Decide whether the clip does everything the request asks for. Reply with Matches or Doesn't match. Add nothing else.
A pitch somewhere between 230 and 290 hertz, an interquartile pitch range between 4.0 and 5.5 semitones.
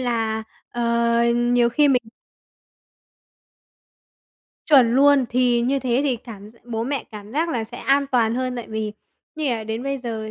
Doesn't match